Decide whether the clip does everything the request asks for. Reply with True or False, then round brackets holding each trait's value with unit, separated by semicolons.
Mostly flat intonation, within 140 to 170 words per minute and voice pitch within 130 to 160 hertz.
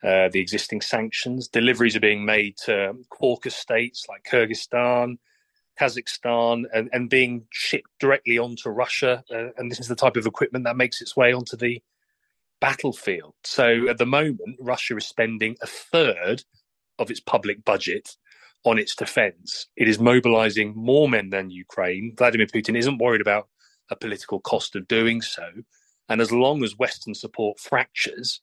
False (2.1 semitones; 165 wpm; 120 Hz)